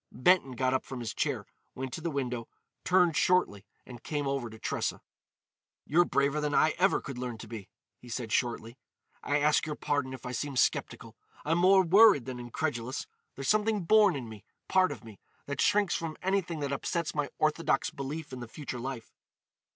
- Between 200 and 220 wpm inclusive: No, average, 185 wpm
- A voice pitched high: No, medium, 140 Hz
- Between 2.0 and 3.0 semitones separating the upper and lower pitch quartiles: No, average, 5.0 semitones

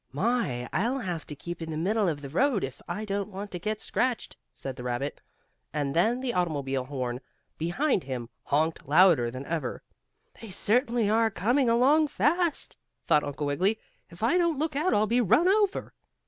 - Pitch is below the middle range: No, high, 190 Hz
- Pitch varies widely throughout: Yes, wide, 9.0 semitones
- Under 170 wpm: No, average, 185 wpm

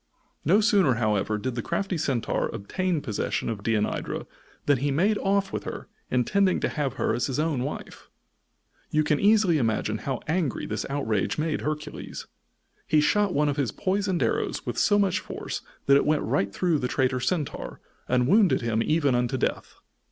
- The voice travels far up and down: Yes, wide, 6.8 semitones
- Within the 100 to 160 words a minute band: No, average, 180 wpm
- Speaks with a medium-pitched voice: Yes, medium, 145 Hz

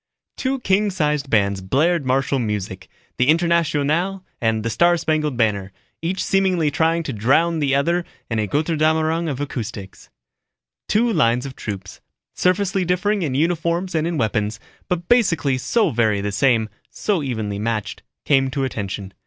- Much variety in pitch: Yes, wide, 7.2 semitones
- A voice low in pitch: No, medium, 145 Hz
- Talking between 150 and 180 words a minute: Yes, average, 155 wpm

